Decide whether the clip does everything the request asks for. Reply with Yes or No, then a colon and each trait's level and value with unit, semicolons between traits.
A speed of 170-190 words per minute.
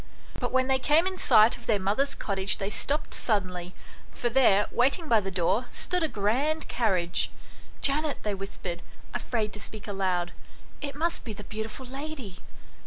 Yes: average, 175 wpm